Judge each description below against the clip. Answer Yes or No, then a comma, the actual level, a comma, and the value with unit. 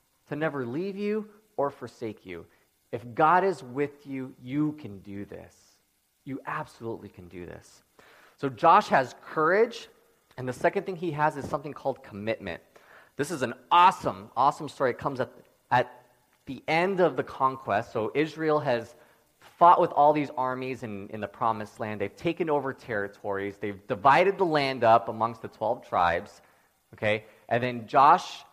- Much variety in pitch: Yes, wide, 6.0 semitones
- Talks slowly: No, average, 170 wpm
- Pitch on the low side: Yes, low, 130 Hz